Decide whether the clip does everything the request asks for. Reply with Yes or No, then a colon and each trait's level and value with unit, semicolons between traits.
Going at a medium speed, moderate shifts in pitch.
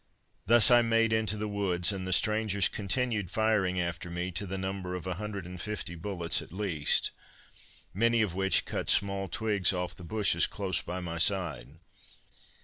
Yes: average, 160 wpm; average, 3.1 semitones